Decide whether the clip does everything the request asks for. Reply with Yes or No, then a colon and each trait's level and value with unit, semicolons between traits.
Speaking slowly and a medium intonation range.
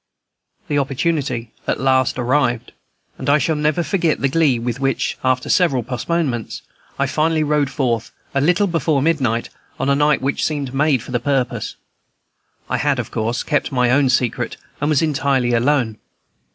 No: average, 165 wpm; average, 3.3 semitones